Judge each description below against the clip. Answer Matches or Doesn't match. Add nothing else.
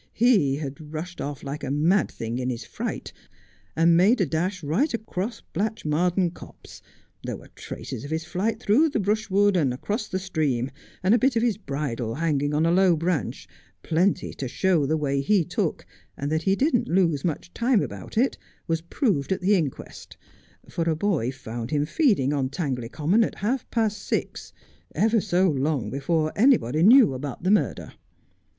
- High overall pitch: Doesn't match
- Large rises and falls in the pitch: Matches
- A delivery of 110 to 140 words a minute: Doesn't match